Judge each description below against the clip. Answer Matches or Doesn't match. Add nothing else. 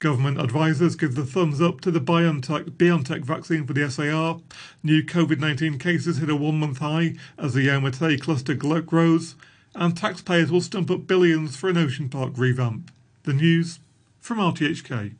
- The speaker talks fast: Doesn't match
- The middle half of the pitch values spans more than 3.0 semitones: Doesn't match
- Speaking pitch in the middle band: Matches